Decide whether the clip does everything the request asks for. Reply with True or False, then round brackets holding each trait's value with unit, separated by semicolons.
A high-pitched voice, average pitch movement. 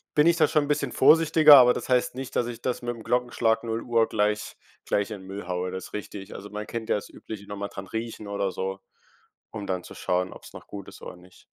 False (110 Hz; 3.8 semitones)